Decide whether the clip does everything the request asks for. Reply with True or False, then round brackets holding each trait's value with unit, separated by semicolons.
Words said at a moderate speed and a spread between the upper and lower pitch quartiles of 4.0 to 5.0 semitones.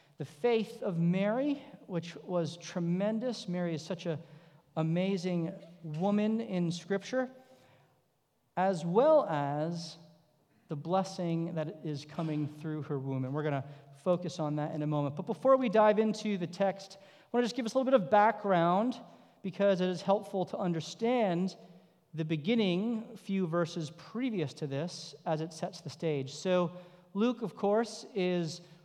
True (160 wpm; 4.5 semitones)